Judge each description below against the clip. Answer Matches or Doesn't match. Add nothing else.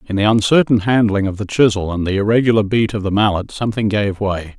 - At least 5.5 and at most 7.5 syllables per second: Matches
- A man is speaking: Matches